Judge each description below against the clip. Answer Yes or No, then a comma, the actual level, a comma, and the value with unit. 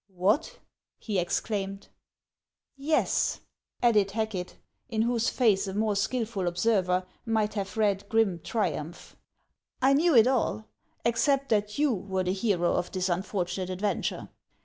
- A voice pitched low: No, high, 210 Hz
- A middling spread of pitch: Yes, average, 3.6 semitones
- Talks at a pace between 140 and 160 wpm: Yes, average, 150 wpm